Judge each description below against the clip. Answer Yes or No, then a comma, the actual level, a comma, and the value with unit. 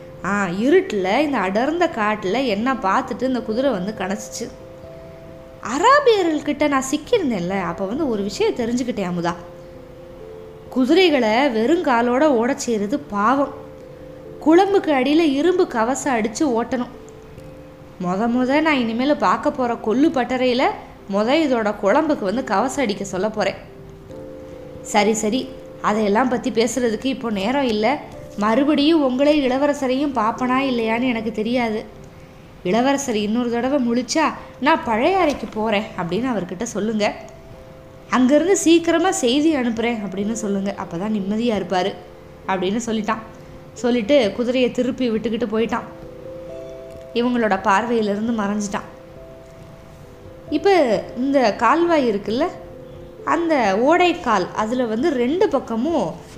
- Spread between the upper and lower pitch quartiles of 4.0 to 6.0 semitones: Yes, average, 5.2 semitones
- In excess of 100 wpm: Yes, average, 110 wpm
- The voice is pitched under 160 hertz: No, high, 240 Hz